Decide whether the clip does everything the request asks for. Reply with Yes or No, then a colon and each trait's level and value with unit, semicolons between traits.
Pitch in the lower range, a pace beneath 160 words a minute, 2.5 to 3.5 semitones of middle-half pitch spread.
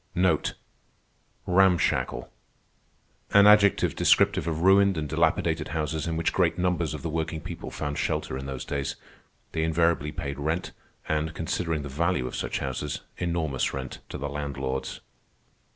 Yes: very low, 80 Hz; average, 140 wpm; average, 2.8 semitones